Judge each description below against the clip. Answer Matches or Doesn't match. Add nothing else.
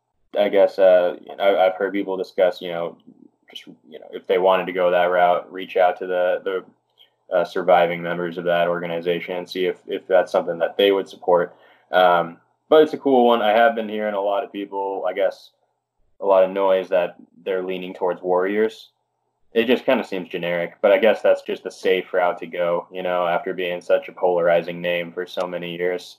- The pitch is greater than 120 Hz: Doesn't match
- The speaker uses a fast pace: Matches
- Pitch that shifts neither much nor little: Doesn't match